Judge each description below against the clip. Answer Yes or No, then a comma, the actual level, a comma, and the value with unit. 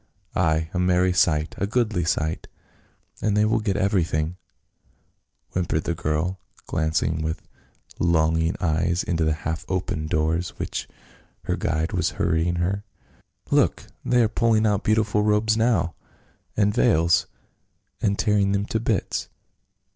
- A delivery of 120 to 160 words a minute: Yes, average, 155 wpm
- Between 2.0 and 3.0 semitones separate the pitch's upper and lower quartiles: No, average, 4.4 semitones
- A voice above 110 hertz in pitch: No, very low, 90 Hz